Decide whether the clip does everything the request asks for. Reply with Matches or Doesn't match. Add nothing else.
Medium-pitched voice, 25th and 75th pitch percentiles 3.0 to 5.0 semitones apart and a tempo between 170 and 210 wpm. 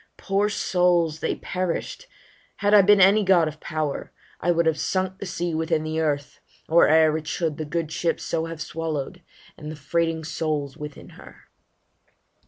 Doesn't match